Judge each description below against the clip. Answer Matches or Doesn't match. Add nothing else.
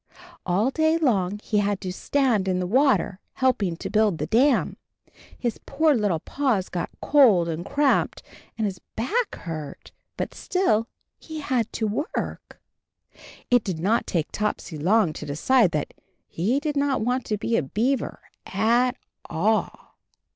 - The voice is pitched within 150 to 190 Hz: Doesn't match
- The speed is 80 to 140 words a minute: Doesn't match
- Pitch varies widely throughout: Matches